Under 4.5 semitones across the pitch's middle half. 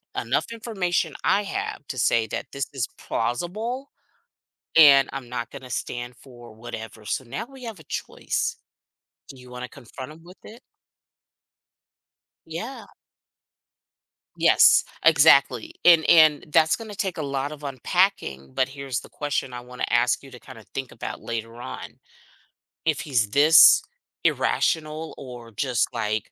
No: average, 5.3 semitones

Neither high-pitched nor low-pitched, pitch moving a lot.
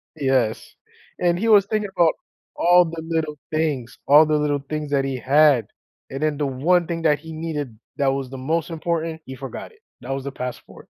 No: medium, 150 Hz; average, 3.4 semitones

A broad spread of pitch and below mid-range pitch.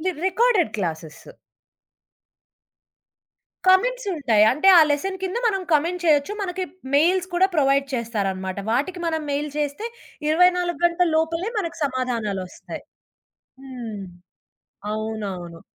No: wide, 8.1 semitones; very high, 300 Hz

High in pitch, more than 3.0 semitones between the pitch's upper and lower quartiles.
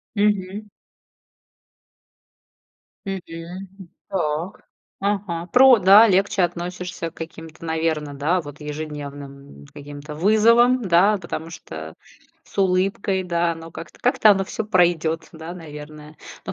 No: medium, 170 Hz; average, 4.0 semitones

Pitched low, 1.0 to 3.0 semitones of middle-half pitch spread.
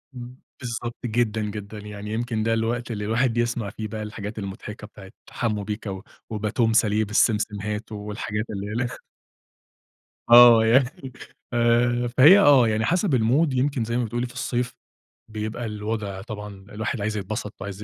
Yes: low, 110 Hz; narrow, 2.4 semitones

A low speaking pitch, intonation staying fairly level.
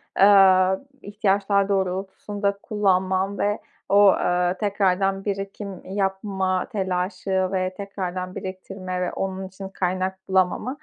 No: high, 190 Hz; narrow, 1.2 semitones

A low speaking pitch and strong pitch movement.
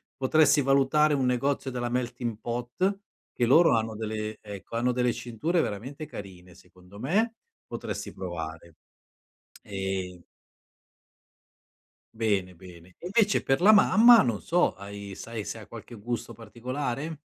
Yes: low, 120 Hz; wide, 5.7 semitones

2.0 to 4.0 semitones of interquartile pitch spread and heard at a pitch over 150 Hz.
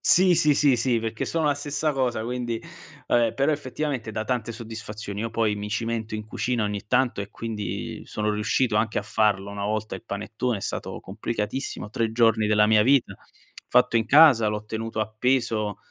No: average, 2.9 semitones; low, 115 Hz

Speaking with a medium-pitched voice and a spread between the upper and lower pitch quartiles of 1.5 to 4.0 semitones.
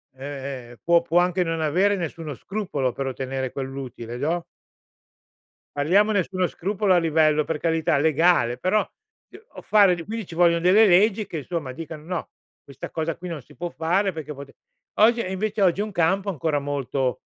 No: medium, 165 Hz; average, 4.6 semitones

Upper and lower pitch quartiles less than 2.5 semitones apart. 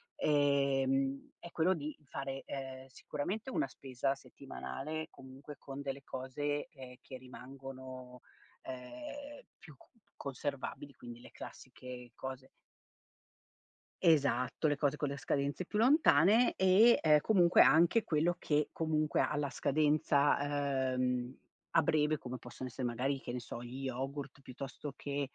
No: average, 2.8 semitones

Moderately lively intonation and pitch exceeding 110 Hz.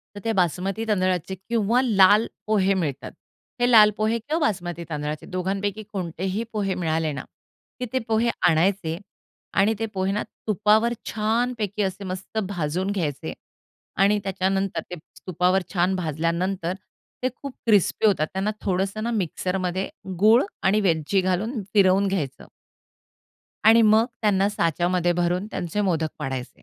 Yes: average, 3.3 semitones; high, 190 Hz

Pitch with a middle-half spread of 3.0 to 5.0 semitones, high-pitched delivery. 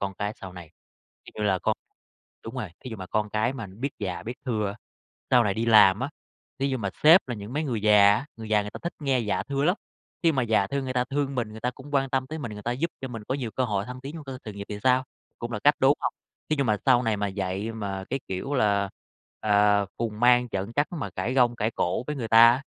No: average, 4.3 semitones; low, 115 Hz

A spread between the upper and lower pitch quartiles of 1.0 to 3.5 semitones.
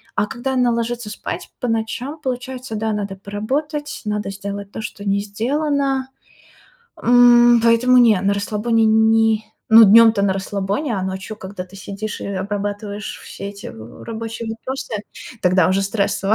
Yes: average, 3.1 semitones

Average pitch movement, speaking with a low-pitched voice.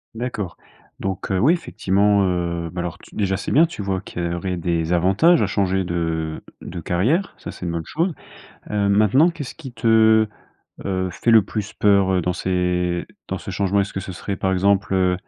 Yes: average, 3.1 semitones; very low, 95 Hz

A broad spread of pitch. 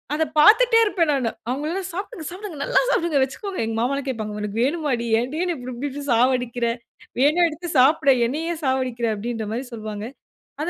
Yes: wide, 5.7 semitones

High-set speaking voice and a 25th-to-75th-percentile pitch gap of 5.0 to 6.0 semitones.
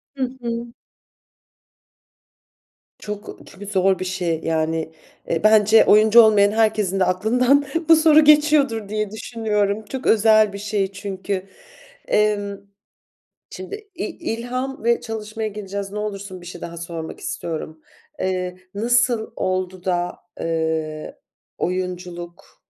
No: high, 205 Hz; average, 3.4 semitones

